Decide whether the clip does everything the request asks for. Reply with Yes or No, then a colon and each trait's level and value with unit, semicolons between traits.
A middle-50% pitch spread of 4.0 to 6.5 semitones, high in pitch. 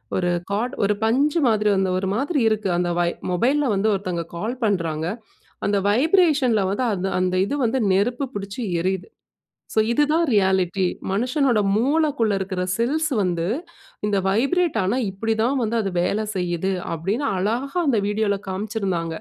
Yes: average, 5.0 semitones; high, 210 Hz